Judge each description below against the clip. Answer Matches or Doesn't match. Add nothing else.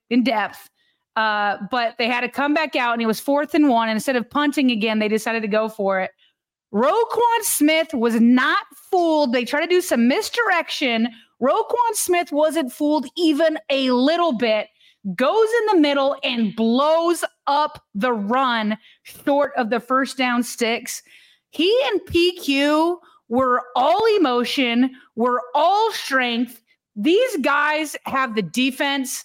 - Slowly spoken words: Doesn't match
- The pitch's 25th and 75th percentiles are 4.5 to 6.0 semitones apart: Matches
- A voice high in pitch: Matches